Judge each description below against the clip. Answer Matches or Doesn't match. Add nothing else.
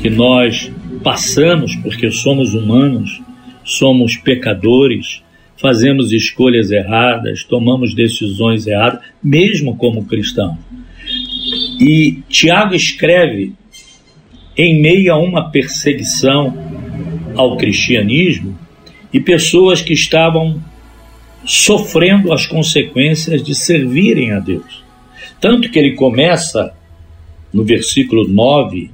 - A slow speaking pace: Matches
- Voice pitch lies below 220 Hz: Matches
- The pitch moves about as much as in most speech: Doesn't match